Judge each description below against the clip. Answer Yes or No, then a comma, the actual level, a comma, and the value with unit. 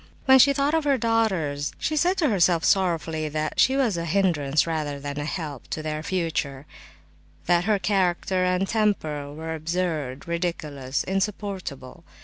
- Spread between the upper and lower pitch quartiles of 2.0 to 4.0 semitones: No, average, 4.9 semitones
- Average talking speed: Yes, average, 155 wpm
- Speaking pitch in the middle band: Yes, medium, 170 Hz